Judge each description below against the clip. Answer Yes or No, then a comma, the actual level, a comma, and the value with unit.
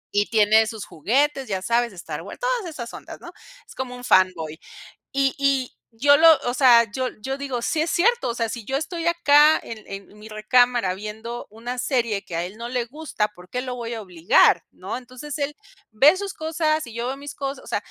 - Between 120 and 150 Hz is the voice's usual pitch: No, high, 245 Hz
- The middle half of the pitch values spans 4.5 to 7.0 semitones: Yes, average, 4.9 semitones